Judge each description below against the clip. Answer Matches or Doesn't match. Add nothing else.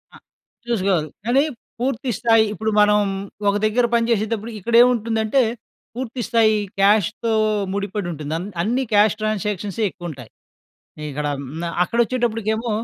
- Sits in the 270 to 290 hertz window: Doesn't match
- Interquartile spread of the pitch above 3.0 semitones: Doesn't match